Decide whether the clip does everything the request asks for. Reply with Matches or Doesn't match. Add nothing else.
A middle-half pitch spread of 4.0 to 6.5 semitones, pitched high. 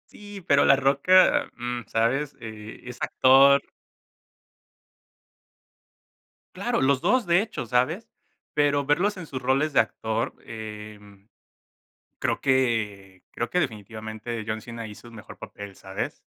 Doesn't match